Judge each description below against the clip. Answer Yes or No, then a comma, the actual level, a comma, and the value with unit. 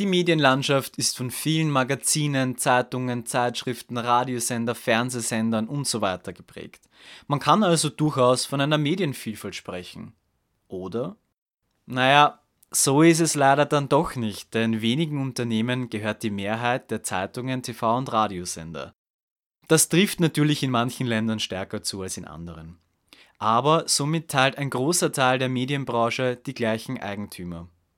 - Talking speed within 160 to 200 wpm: No, average, 135 wpm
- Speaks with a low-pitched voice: Yes, low, 125 Hz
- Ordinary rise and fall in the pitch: Yes, average, 4.4 semitones